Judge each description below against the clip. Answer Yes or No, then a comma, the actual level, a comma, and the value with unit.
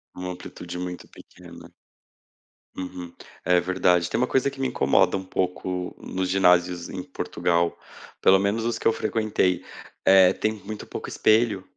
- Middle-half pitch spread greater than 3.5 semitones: No, average, 2.7 semitones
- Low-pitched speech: Yes, very low, 95 Hz